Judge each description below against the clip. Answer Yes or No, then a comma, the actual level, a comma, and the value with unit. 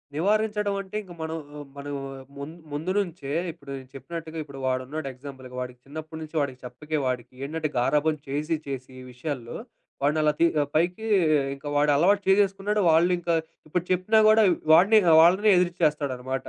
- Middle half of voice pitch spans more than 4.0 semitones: Yes, average, 4.5 semitones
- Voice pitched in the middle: Yes, medium, 155 Hz